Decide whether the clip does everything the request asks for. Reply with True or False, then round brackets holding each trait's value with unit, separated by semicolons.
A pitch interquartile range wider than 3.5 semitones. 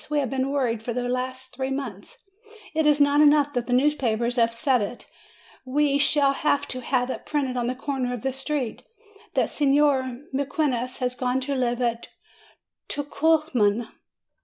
False (2.5 semitones)